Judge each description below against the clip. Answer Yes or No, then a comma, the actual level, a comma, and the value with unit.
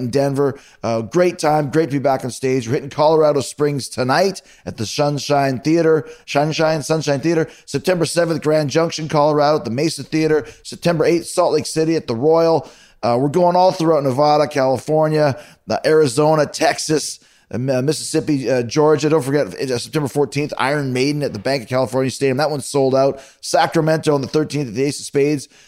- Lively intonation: No, average, 2.7 semitones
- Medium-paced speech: Yes, average, 190 wpm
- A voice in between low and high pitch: Yes, medium, 145 Hz